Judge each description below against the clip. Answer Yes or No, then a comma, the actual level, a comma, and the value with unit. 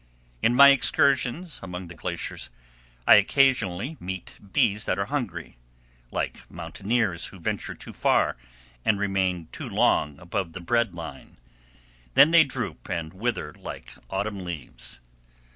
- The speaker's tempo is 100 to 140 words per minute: Yes, slow, 135 wpm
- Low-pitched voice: Yes, low, 100 Hz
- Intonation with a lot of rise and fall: Yes, wide, 5.9 semitones